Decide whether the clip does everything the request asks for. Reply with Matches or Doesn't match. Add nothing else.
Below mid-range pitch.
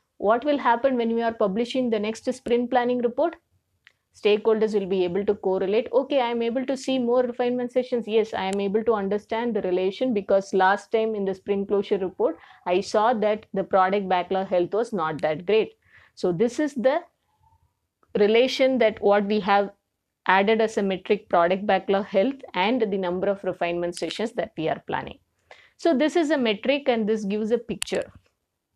Doesn't match